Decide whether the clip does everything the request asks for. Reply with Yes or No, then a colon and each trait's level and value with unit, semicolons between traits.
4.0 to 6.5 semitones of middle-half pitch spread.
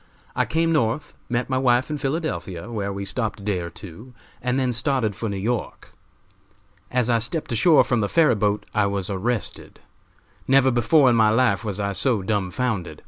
Yes: average, 4.3 semitones